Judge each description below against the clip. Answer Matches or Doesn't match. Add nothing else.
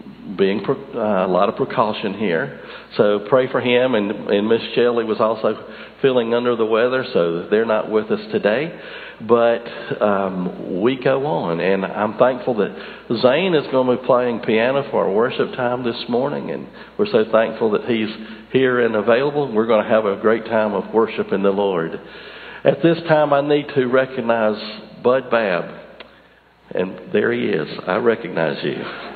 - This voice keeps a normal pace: Matches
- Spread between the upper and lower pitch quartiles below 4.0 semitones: Matches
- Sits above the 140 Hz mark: Doesn't match